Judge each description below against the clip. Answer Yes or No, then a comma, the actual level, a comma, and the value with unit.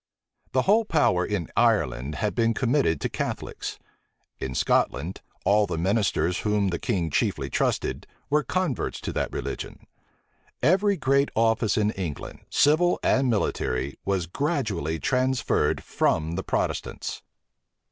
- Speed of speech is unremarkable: No, slow, 130 wpm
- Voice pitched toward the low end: Yes, low, 105 Hz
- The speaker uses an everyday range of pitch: No, wide, 8.1 semitones